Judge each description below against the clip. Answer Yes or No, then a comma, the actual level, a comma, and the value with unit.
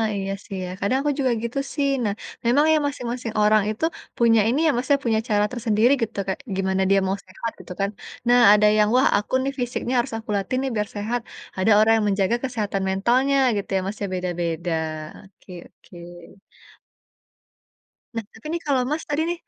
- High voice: Yes, high, 220 Hz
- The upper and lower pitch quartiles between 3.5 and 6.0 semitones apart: Yes, average, 4.2 semitones